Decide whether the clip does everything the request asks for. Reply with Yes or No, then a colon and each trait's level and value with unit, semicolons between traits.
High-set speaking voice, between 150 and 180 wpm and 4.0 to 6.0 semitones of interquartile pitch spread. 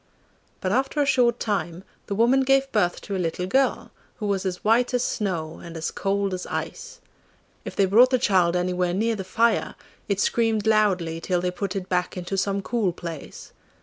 No: high, 195 Hz; average, 195 wpm; average, 4.3 semitones